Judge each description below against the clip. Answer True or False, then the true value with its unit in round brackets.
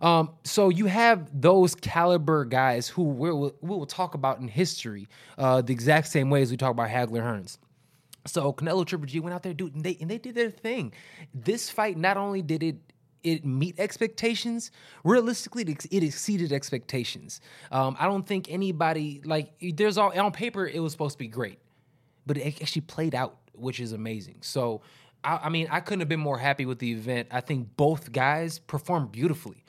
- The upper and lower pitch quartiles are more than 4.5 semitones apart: True (5.3 semitones)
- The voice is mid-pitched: True (155 Hz)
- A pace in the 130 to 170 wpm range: False (200 wpm)